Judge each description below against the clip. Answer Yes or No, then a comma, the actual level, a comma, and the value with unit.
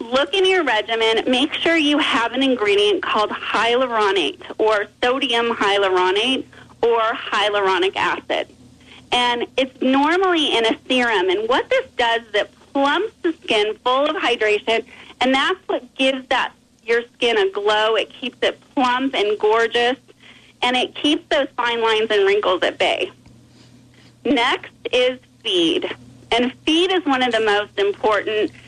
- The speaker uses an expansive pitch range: Yes, wide, 7.8 semitones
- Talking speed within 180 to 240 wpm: No, average, 150 wpm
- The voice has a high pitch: Yes, very high, 260 Hz